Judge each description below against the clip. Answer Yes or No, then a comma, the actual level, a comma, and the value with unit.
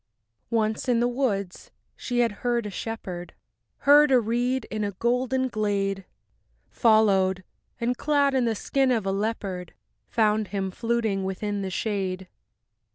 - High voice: Yes, high, 220 Hz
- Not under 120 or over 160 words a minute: Yes, average, 150 wpm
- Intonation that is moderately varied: Yes, average, 3.7 semitones